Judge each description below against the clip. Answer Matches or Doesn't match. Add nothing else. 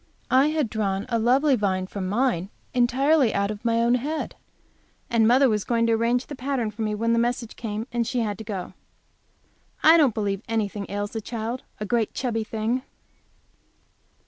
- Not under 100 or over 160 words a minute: Doesn't match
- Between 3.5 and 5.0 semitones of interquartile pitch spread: Doesn't match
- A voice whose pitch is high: Matches